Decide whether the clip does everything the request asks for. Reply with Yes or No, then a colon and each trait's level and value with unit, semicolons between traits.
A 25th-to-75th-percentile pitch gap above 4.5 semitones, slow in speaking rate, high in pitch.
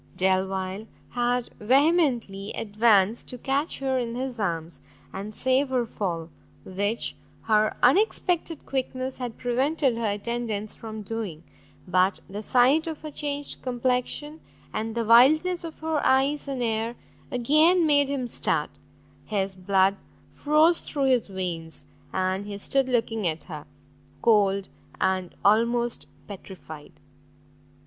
Yes: average, 5.2 semitones; slow, 125 wpm; high, 235 Hz